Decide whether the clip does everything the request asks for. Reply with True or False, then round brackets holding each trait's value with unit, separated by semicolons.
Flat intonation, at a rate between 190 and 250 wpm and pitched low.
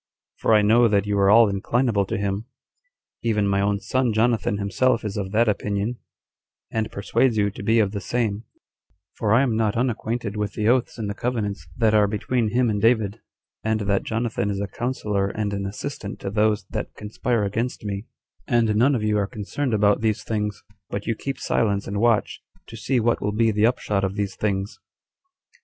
True (2.3 semitones; 200 wpm; 105 Hz)